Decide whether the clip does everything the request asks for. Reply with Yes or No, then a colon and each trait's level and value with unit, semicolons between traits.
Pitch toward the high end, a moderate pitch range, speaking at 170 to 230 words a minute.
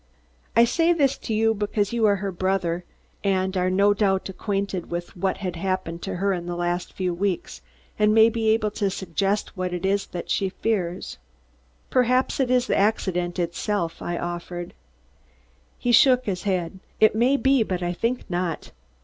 Yes: high, 195 Hz; average, 3.6 semitones; average, 175 wpm